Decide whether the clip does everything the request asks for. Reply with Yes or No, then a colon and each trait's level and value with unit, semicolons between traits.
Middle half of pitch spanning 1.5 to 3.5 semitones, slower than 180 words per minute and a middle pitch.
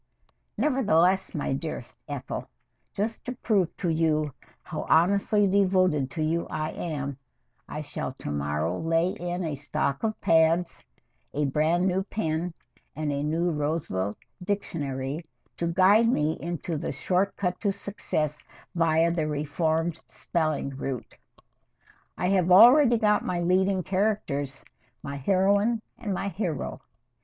No: average, 4.3 semitones; slow, 135 wpm; medium, 170 Hz